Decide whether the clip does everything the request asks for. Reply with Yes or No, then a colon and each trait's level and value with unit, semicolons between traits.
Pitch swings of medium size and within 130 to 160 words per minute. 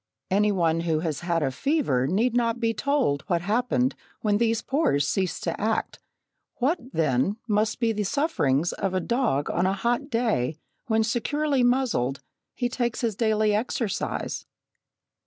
No: wide, 6.2 semitones; average, 155 wpm